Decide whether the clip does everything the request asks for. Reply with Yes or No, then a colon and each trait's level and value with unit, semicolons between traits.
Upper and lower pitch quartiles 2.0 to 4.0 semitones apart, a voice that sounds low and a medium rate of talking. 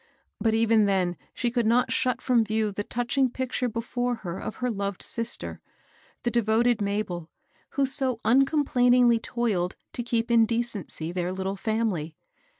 No: average, 3.4 semitones; high, 230 Hz; average, 160 wpm